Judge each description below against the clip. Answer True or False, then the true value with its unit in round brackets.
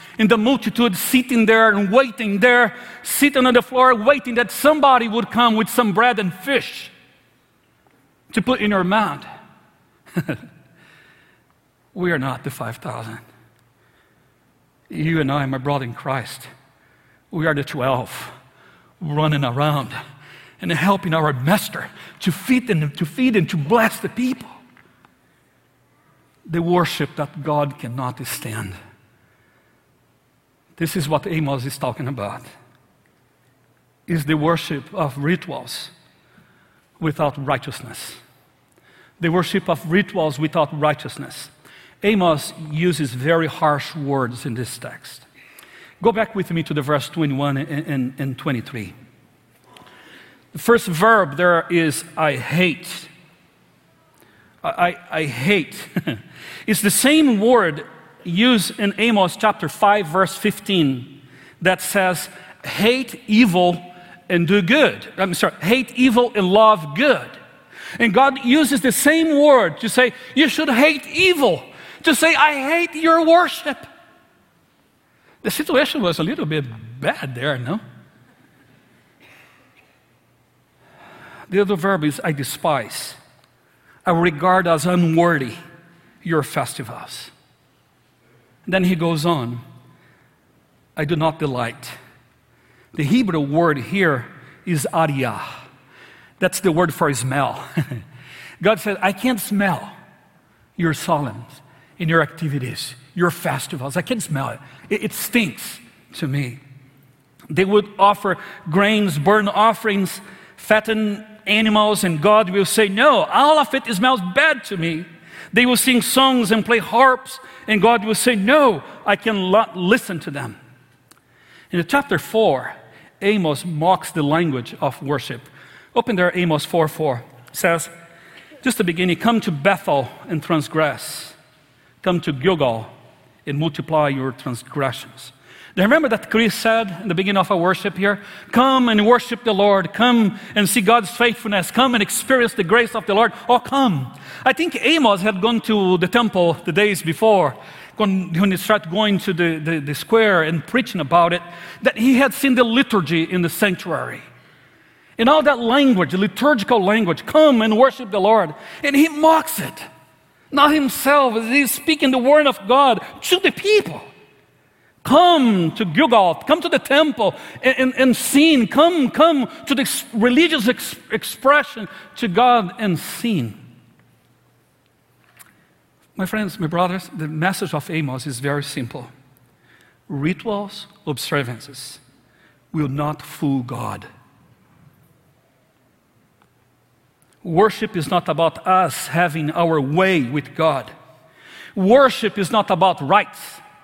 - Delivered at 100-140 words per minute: True (135 wpm)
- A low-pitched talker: False (180 Hz)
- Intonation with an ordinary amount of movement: False (7.2 semitones)